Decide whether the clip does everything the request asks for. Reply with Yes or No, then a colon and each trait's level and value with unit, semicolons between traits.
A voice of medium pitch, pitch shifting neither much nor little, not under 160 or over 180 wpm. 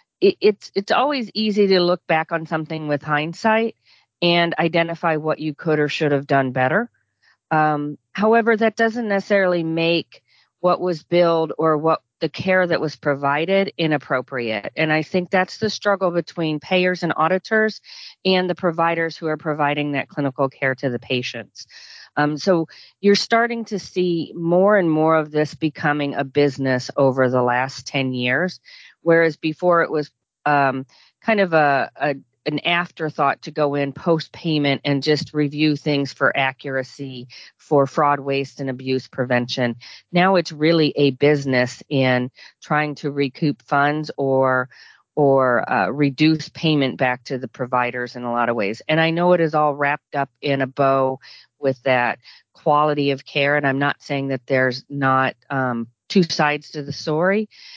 Yes: medium, 150 Hz; average, 3.9 semitones; average, 165 wpm